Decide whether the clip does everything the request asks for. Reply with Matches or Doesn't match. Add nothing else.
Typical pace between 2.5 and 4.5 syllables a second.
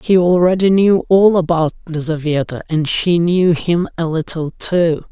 Matches